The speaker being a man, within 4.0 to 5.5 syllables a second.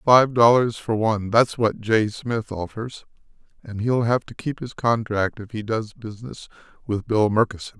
Yes: male; 4.6 syllables/s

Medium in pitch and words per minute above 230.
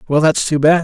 Yes: medium, 155 Hz; fast, 290 wpm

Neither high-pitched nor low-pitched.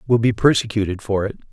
No: low, 110 Hz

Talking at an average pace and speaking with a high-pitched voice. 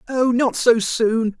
Yes: average, 170 wpm; high, 235 Hz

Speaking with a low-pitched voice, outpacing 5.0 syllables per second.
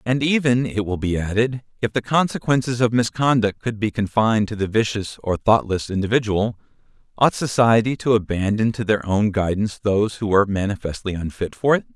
Yes: low, 110 Hz; 5.5 syllables/s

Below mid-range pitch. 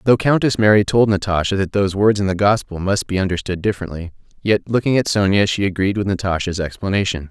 Yes: low, 100 Hz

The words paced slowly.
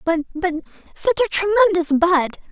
Yes: slow, 95 wpm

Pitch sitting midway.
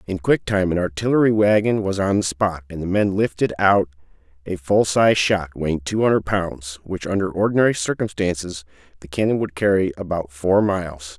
No: very low, 90 Hz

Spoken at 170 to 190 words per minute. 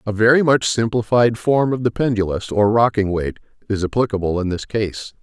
Yes: average, 185 wpm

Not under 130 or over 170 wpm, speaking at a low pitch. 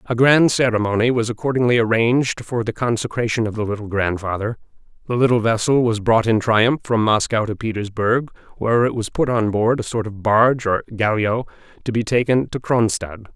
No: average, 185 wpm; low, 115 Hz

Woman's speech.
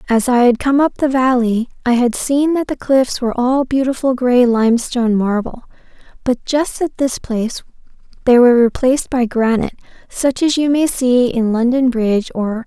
Yes: female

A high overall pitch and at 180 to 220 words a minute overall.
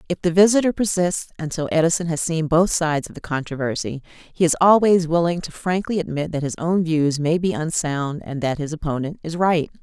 No: medium, 165 Hz; average, 200 wpm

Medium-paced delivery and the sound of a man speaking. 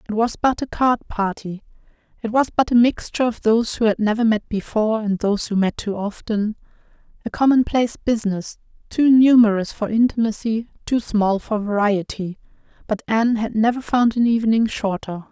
No: average, 170 wpm; female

